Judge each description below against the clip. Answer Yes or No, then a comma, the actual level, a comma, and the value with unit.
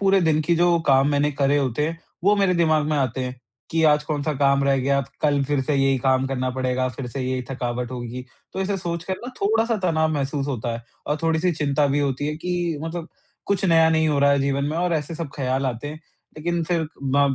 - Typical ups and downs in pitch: Yes, average, 3.5 semitones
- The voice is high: No, medium, 145 Hz